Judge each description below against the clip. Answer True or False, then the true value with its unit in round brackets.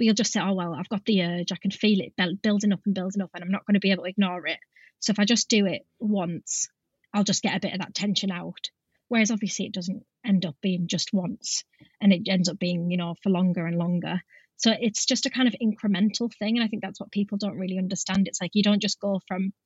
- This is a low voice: False (195 Hz)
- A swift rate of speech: True (270 wpm)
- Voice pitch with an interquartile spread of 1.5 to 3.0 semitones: True (2.4 semitones)